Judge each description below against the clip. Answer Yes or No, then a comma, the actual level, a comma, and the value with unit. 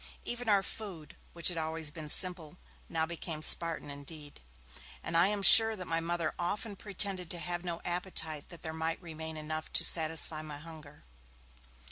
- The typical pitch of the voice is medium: Yes, medium, 165 Hz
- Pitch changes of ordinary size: No, narrow, 2.3 semitones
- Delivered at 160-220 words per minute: Yes, average, 170 wpm